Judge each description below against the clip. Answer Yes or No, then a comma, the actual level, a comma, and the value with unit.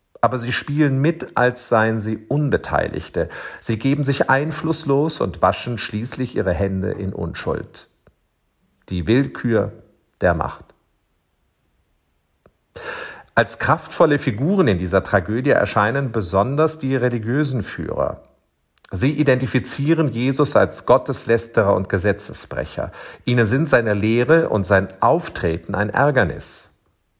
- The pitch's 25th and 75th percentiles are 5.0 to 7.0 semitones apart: Yes, wide, 5.6 semitones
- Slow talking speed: Yes, slow, 110 wpm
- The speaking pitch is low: Yes, low, 120 Hz